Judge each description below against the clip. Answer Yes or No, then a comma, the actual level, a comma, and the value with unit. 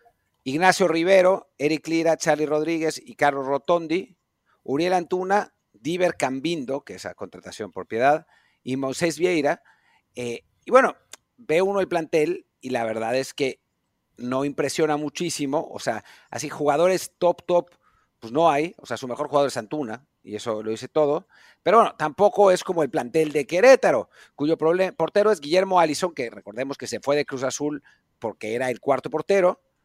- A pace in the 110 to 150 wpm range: No, average, 170 wpm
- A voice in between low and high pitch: Yes, medium, 155 Hz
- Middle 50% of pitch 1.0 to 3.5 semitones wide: No, average, 4.7 semitones